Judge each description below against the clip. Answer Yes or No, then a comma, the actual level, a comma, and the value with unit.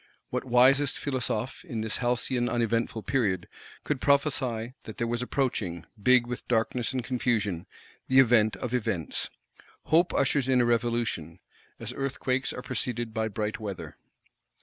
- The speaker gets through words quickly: No, average, 140 wpm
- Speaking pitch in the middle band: No, low, 120 Hz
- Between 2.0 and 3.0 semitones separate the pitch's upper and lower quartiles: Yes, narrow, 2.6 semitones